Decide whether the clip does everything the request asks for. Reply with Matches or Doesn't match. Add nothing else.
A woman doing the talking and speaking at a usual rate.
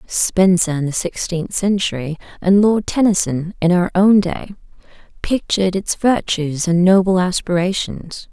Doesn't match